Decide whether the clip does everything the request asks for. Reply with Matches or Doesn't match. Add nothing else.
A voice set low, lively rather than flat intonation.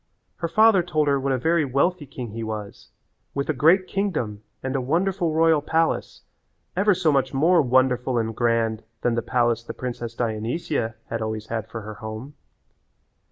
Matches